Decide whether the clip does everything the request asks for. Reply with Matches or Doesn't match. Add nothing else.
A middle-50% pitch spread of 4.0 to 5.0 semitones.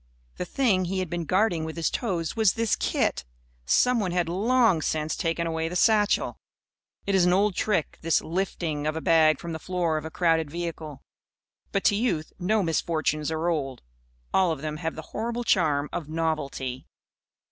Doesn't match